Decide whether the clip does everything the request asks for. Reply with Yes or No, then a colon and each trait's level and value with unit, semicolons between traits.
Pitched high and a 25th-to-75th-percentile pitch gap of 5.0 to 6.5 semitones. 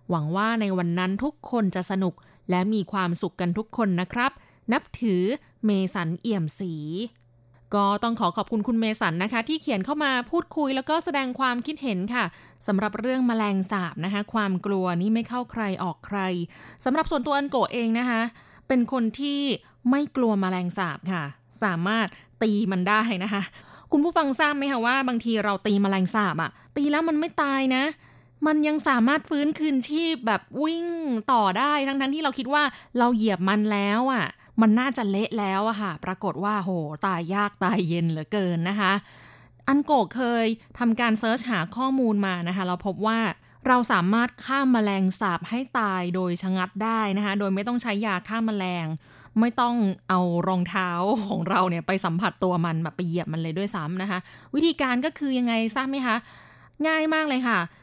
Yes: high, 215 Hz; average, 5.3 semitones